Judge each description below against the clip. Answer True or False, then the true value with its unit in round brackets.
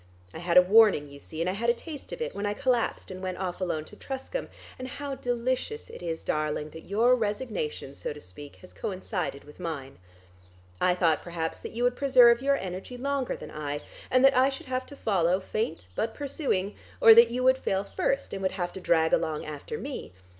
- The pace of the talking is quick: True (220 wpm)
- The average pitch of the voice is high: True (200 Hz)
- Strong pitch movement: True (7.2 semitones)